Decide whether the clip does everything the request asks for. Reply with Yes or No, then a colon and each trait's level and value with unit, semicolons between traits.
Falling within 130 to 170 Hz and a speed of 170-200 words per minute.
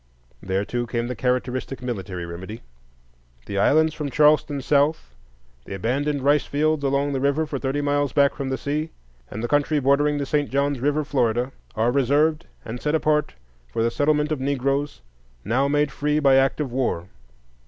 Yes: medium, 140 Hz; average, 175 wpm